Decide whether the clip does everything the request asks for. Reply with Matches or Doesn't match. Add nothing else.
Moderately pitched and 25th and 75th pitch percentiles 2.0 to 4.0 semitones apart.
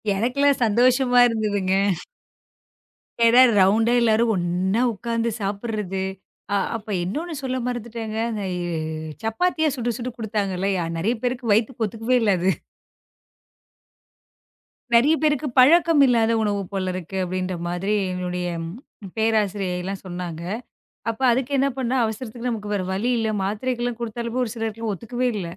Doesn't match